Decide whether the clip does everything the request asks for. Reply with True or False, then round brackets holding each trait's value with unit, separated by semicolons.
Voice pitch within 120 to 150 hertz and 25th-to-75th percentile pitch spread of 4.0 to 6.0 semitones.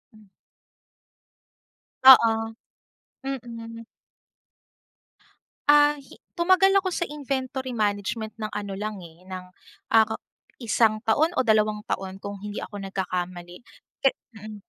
False (220 Hz; 4.6 semitones)